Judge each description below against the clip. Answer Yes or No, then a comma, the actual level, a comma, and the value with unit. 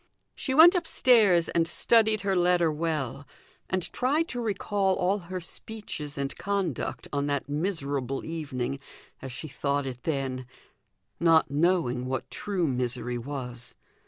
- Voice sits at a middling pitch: Yes, medium, 160 Hz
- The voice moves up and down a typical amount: No, wide, 6.1 semitones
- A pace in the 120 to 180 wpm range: Yes, slow, 135 wpm